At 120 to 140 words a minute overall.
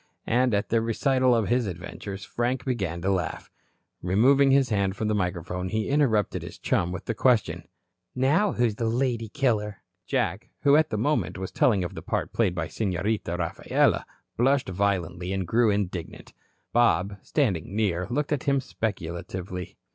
No: average, 165 wpm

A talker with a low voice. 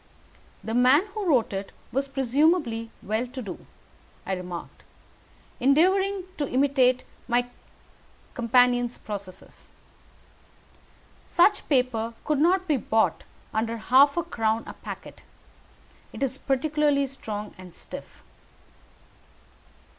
No: very high, 255 Hz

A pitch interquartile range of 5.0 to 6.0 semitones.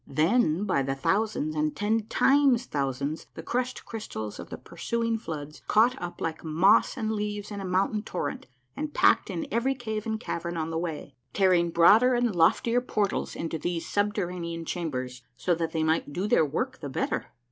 Yes: wide, 5.6 semitones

